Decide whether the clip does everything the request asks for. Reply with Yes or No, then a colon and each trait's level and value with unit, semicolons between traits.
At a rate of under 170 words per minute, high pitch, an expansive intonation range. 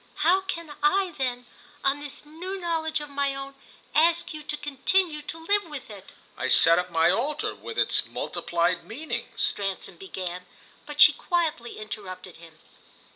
Yes: average, 160 wpm; very high, 290 Hz; wide, 9.0 semitones